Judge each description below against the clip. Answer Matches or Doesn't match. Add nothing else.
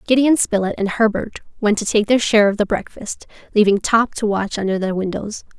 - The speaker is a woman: Matches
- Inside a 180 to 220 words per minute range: Matches